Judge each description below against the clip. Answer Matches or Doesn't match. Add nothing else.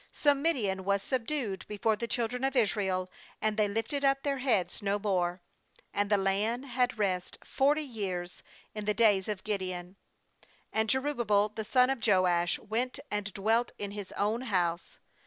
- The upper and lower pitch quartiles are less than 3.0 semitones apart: Doesn't match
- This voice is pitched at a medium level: Doesn't match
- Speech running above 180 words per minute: Doesn't match